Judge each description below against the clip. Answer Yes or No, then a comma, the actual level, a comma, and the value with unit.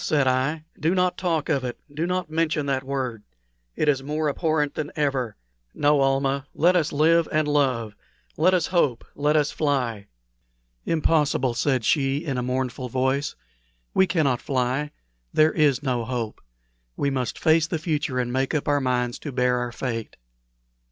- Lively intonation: No, average, 3.3 semitones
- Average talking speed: Yes, average, 170 wpm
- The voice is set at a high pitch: No, medium, 140 Hz